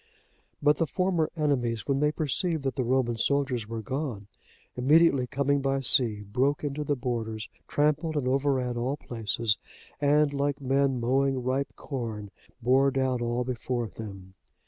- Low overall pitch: Yes, low, 130 Hz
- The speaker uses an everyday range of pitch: Yes, average, 3.1 semitones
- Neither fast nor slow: Yes, average, 150 wpm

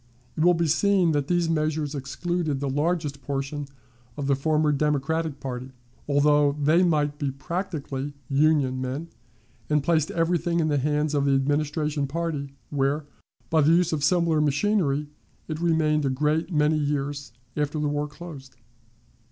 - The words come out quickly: No, average, 155 wpm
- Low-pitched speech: No, medium, 150 Hz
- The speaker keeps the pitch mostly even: Yes, narrow, 2.3 semitones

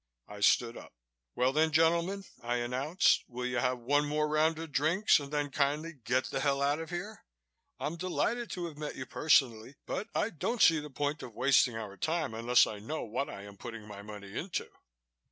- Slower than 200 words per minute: No, fast, 205 wpm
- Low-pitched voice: No, medium, 145 Hz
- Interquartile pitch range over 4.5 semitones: Yes, average, 4.9 semitones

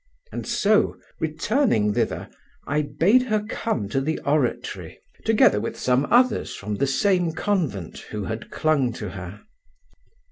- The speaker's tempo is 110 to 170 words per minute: Yes, average, 140 wpm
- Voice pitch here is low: No, medium, 150 Hz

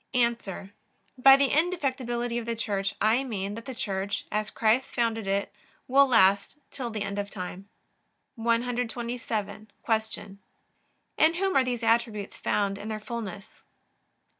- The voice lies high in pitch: Yes, high, 230 Hz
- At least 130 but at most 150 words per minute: Yes, average, 140 wpm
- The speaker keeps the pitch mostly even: No, average, 3.4 semitones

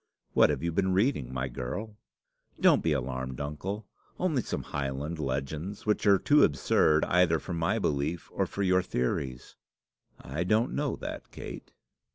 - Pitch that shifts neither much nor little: No, wide, 6.4 semitones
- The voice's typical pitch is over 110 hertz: No, very low, 80 Hz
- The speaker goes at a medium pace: Yes, average, 160 wpm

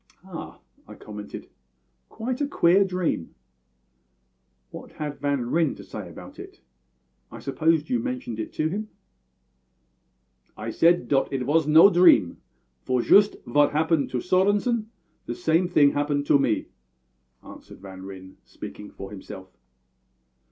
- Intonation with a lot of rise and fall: Yes, wide, 7.2 semitones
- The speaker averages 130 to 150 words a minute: Yes, slow, 135 wpm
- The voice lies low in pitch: No, medium, 150 Hz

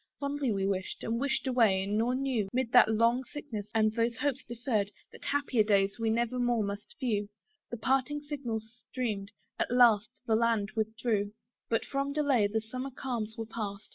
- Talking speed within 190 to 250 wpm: No, average, 175 wpm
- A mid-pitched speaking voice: No, high, 230 Hz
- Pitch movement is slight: No, average, 3.1 semitones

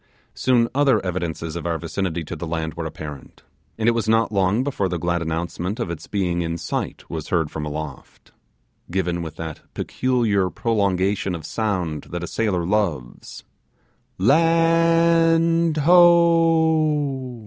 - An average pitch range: No, wide, 8.7 semitones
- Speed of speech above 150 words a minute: No, average, 145 wpm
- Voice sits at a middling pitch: No, very low, 95 Hz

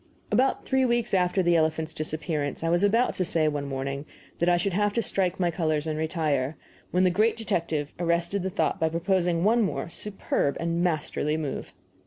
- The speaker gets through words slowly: No, average, 195 wpm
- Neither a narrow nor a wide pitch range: Yes, average, 3.4 semitones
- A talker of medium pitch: Yes, medium, 170 Hz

